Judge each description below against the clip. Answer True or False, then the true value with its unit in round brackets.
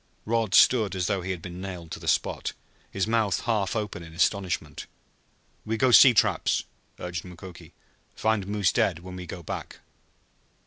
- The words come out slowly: False (170 wpm)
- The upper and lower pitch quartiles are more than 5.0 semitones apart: False (3.4 semitones)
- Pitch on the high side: False (95 Hz)